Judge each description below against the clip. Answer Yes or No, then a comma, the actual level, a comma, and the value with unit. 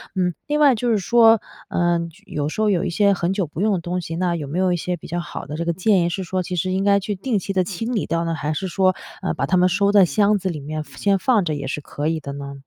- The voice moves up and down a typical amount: Yes, average, 3.3 semitones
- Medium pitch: Yes, medium, 180 Hz